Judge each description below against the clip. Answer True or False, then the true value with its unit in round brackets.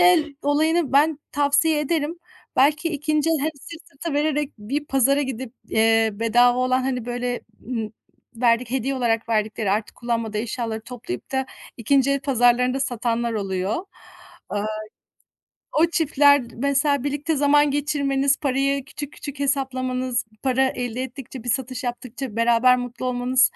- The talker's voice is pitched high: True (260 Hz)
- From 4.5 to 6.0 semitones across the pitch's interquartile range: False (3.2 semitones)